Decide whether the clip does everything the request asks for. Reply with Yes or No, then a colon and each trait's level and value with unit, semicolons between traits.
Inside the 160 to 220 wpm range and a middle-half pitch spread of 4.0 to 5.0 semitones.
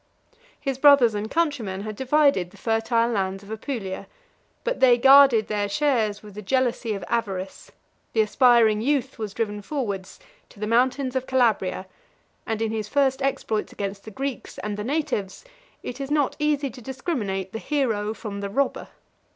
Yes: average, 165 wpm; average, 4.5 semitones